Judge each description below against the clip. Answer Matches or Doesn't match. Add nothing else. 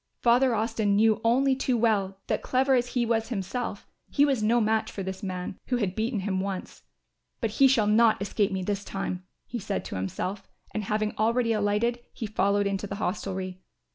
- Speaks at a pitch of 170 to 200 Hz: Doesn't match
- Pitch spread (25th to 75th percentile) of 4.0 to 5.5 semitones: Doesn't match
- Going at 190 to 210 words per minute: Matches